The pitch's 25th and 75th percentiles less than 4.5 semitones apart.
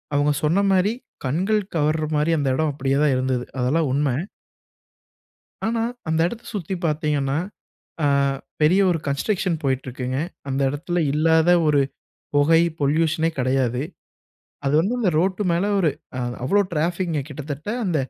Yes: average, 3.8 semitones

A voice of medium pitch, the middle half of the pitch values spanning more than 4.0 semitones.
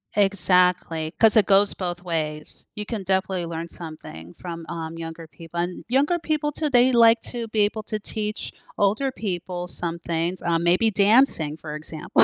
Yes: medium, 180 Hz; average, 4.6 semitones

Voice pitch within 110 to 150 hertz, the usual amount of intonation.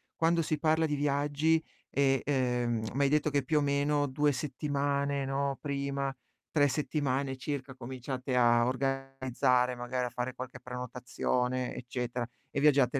No: low, 135 Hz; narrow, 2.2 semitones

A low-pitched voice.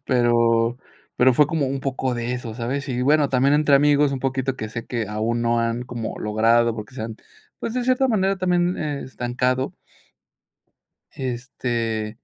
Yes: low, 125 Hz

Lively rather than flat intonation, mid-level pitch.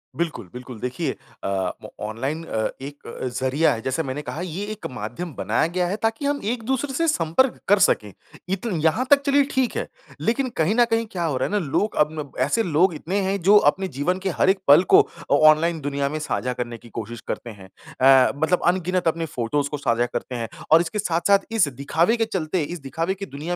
Yes: wide, 6.3 semitones; medium, 165 Hz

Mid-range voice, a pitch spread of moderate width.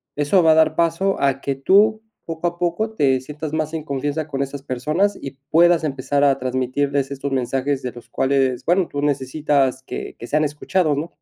Yes: medium, 145 Hz; average, 3.3 semitones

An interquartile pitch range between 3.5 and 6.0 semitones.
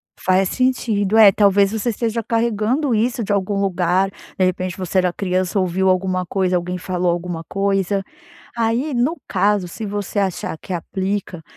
No: average, 2.9 semitones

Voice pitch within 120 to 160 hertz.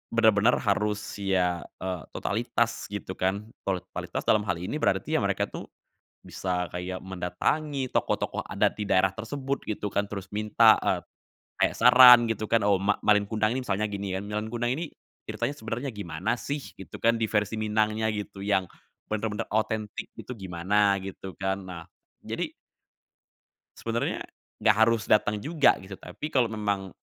No: low, 105 Hz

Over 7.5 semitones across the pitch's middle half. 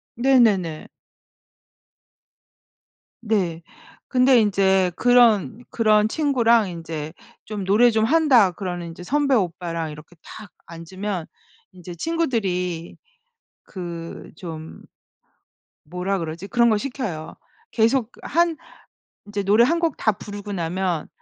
No: wide, 5.4 semitones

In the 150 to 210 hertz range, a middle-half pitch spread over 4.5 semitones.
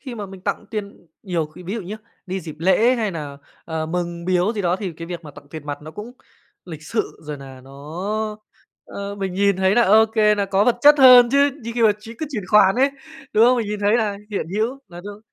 No: high, 200 Hz; average, 4.2 semitones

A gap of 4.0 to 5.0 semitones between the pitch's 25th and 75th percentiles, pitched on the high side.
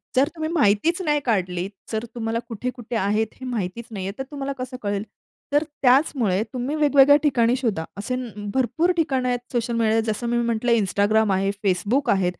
Yes: average, 4.3 semitones; high, 235 Hz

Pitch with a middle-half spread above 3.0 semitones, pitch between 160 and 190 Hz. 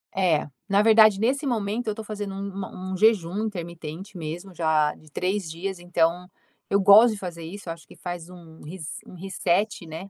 Yes: average, 3.5 semitones; medium, 185 Hz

